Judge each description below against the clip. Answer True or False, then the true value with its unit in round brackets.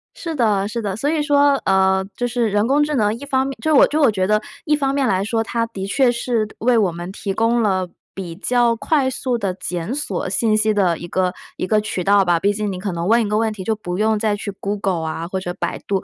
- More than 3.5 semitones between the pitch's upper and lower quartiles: True (4.2 semitones)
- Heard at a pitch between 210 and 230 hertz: True (215 Hz)